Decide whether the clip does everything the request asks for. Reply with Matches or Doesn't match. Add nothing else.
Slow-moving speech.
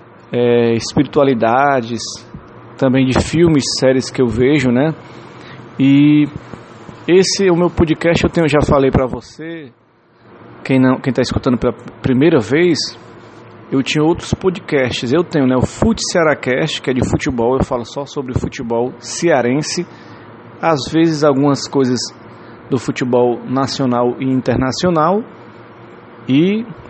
Matches